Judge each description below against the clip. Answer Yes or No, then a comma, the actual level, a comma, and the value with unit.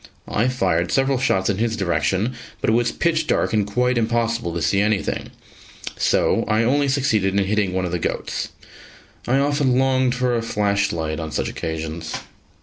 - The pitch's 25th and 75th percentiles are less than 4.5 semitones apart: No, average, 5.1 semitones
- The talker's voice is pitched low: Yes, low, 110 Hz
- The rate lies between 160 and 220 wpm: Yes, average, 180 wpm